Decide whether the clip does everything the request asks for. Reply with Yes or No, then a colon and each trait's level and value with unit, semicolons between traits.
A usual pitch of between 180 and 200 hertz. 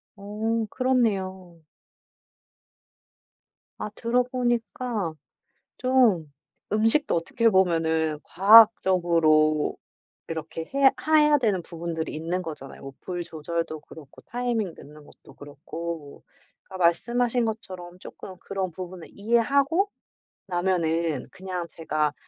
Yes: medium, 185 Hz